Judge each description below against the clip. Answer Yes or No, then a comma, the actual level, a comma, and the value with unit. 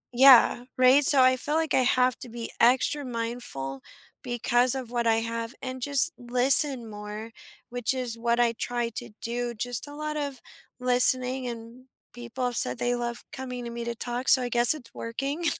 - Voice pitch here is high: Yes, high, 245 Hz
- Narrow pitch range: Yes, narrow, 1.7 semitones